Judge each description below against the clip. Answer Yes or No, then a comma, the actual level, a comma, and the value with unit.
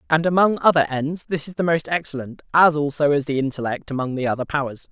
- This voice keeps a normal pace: No, fast, 220 wpm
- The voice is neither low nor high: Yes, medium, 150 Hz